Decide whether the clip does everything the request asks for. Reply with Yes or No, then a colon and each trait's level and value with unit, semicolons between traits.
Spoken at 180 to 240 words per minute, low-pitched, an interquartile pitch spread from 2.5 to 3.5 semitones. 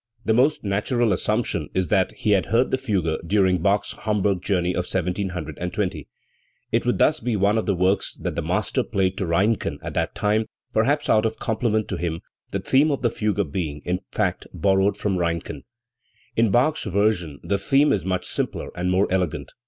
Yes: average, 190 wpm; low, 100 Hz; average, 3.2 semitones